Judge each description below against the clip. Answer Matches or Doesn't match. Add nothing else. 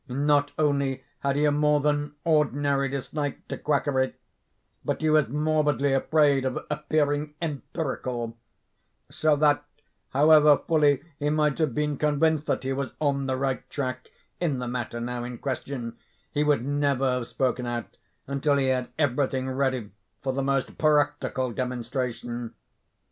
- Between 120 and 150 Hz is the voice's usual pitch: Matches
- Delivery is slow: Doesn't match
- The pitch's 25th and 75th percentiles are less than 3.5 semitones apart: Matches